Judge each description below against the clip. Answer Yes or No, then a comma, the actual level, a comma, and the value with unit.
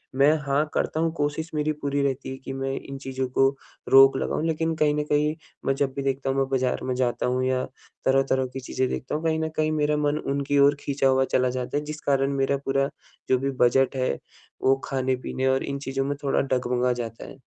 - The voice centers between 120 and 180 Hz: Yes, low, 135 Hz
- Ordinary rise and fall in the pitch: No, narrow, 1.8 semitones